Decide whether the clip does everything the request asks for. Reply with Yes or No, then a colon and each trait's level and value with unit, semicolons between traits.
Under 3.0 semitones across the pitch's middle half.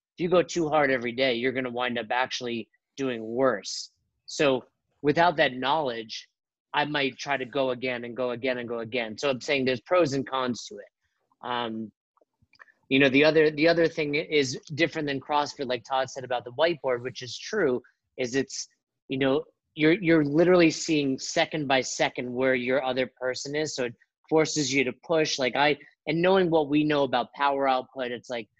No: average, 3.4 semitones